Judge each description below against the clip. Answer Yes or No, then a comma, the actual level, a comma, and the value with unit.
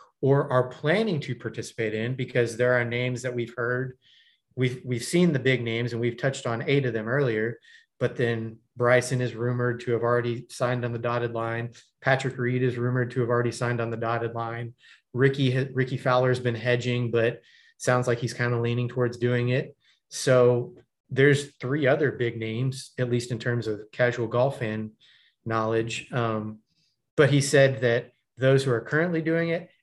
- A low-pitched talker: Yes, low, 125 Hz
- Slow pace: No, average, 190 wpm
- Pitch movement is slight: Yes, narrow, 1.8 semitones